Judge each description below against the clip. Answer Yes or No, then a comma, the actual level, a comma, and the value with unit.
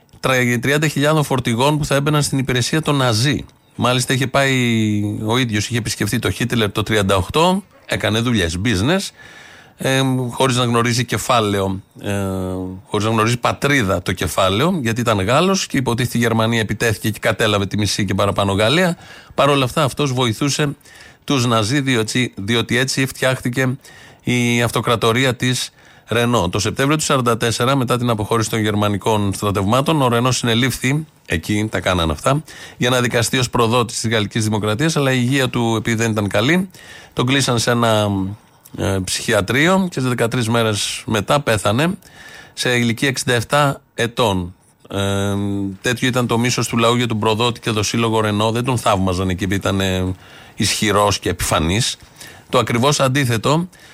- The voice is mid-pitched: No, low, 120 Hz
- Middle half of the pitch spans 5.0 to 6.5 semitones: No, average, 3.7 semitones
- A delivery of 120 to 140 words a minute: No, average, 150 wpm